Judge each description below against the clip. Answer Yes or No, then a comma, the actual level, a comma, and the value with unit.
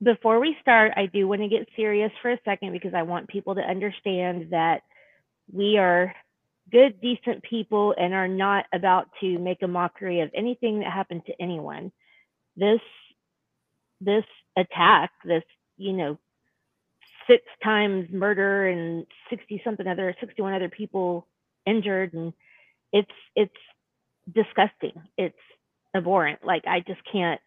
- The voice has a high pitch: Yes, high, 195 Hz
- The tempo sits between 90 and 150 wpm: Yes, average, 140 wpm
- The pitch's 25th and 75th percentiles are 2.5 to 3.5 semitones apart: Yes, average, 2.9 semitones